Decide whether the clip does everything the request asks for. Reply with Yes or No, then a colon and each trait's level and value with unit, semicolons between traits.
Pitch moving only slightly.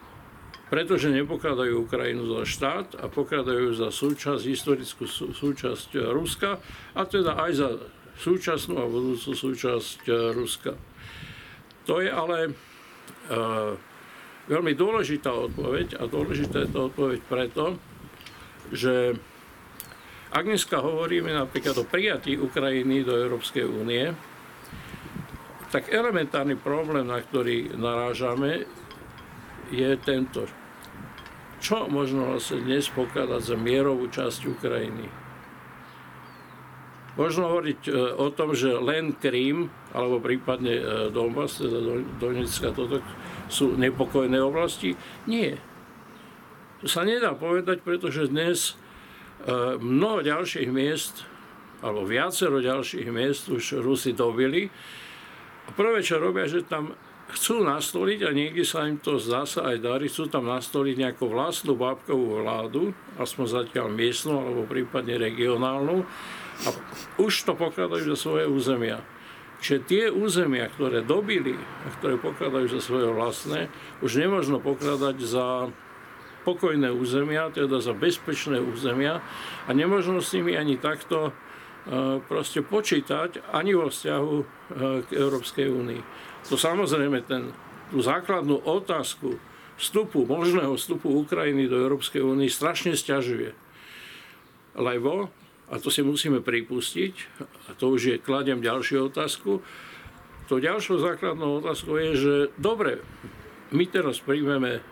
No: average, 3.2 semitones